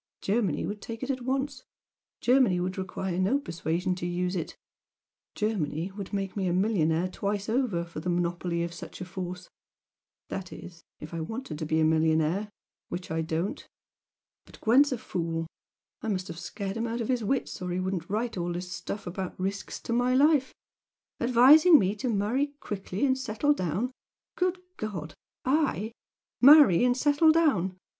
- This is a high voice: Yes, high, 195 Hz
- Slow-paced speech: No, average, 175 wpm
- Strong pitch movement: Yes, wide, 5.9 semitones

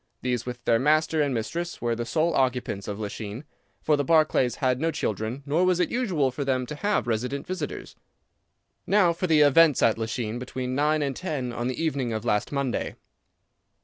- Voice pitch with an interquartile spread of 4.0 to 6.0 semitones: Yes, average, 4.7 semitones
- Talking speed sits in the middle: Yes, average, 190 wpm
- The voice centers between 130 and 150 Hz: Yes, low, 135 Hz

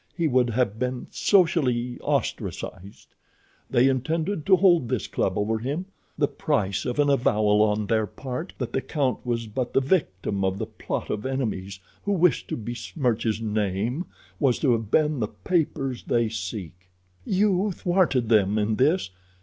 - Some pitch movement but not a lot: No, wide, 5.9 semitones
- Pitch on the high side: No, low, 125 Hz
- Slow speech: No, average, 160 wpm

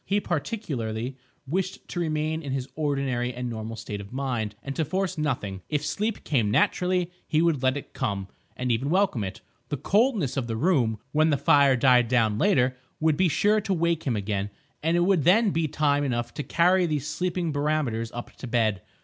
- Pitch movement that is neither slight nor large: No, wide, 5.9 semitones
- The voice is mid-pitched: Yes, medium, 145 Hz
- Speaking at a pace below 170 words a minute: No, average, 195 wpm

